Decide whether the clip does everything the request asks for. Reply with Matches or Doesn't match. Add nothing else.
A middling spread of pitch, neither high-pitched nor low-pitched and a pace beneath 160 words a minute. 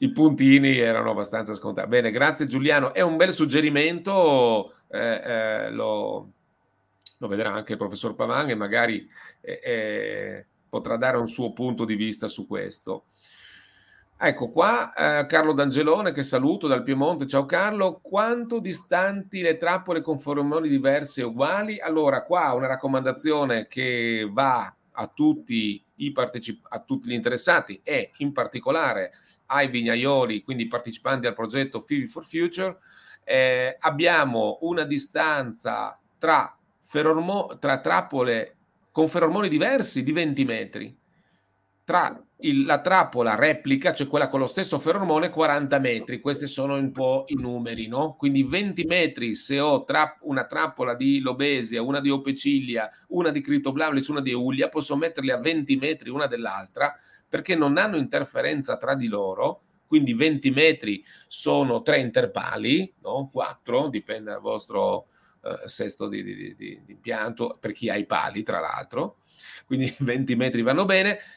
Matches